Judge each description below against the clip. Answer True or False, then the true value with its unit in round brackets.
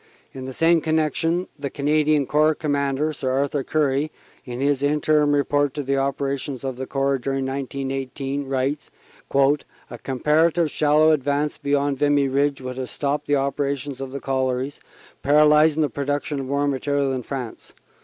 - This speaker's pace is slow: False (170 wpm)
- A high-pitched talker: False (140 Hz)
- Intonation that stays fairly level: True (1.6 semitones)